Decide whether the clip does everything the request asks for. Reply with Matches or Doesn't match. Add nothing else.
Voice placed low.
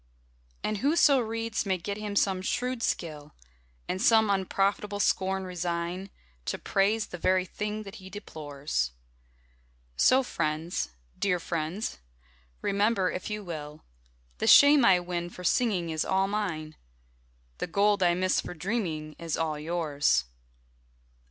Doesn't match